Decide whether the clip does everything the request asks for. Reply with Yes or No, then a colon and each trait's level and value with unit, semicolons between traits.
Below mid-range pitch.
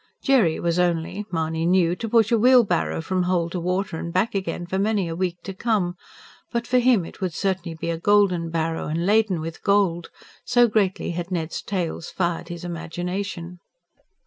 No: medium, 180 Hz